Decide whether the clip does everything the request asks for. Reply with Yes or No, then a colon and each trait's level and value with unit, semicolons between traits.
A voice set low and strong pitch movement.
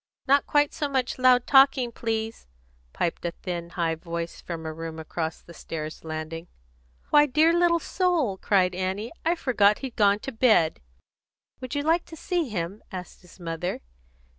No: high, 210 Hz; wide, 8.3 semitones